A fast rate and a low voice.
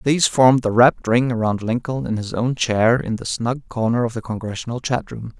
Yes: fast, 220 wpm; low, 120 Hz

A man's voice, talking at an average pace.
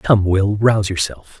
Yes: male; average, 170 wpm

